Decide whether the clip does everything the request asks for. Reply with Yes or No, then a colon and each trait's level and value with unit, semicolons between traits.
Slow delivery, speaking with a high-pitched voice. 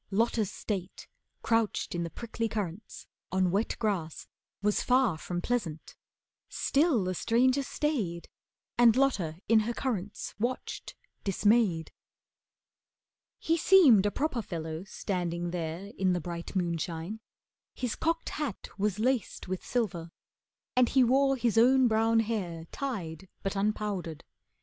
Yes: slow, 130 wpm; high, 210 Hz